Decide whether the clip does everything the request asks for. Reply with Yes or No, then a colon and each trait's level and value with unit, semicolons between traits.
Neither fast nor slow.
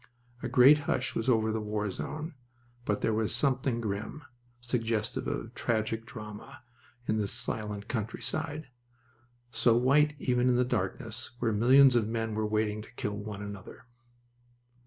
Yes: average, 150 wpm